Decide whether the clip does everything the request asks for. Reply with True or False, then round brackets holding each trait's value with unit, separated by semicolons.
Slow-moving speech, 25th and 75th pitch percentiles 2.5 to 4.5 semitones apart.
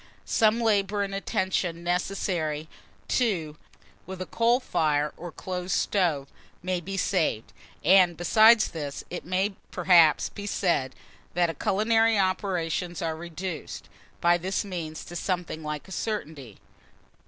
True (130 wpm; 3.4 semitones)